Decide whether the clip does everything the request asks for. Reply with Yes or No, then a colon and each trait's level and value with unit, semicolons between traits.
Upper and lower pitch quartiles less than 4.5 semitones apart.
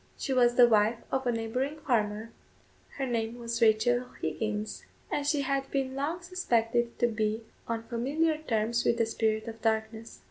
Yes: average, 3.0 semitones